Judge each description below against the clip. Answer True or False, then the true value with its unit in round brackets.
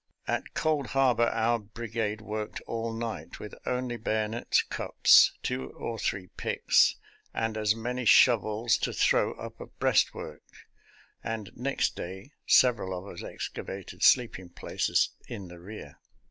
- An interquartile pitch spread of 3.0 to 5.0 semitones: False (2.6 semitones)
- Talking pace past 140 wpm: False (135 wpm)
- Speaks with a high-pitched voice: False (110 Hz)